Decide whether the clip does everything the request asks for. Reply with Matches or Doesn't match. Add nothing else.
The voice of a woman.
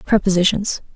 Matches